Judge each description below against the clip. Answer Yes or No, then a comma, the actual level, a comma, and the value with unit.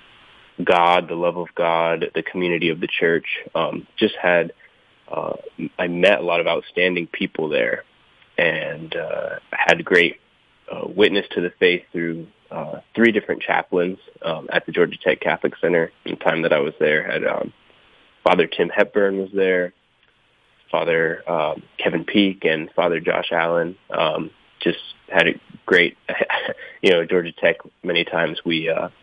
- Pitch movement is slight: Yes, narrow, 1.6 semitones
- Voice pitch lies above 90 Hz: No, very low, 85 Hz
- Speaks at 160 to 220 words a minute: Yes, average, 165 wpm